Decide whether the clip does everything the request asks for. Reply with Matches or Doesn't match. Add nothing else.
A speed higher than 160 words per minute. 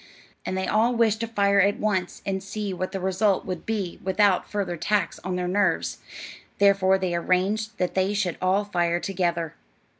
Matches